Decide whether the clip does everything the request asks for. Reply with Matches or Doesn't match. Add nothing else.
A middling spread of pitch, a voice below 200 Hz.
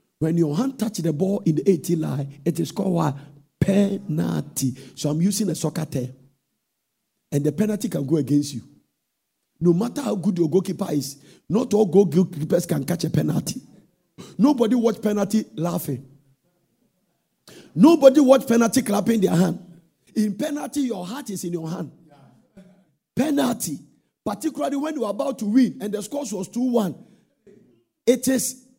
Doesn't match